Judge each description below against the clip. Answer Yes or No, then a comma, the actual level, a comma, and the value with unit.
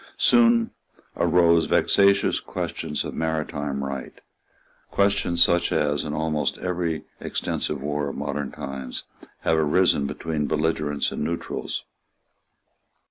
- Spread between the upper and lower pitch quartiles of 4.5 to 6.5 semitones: No, average, 2.8 semitones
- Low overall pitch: Yes, very low, 75 Hz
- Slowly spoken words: Yes, slow, 110 wpm